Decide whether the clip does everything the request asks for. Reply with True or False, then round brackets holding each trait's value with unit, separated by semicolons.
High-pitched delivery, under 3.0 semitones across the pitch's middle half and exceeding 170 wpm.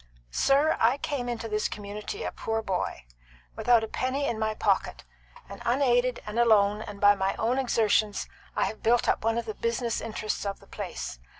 True (225 Hz; 2.5 semitones; 190 wpm)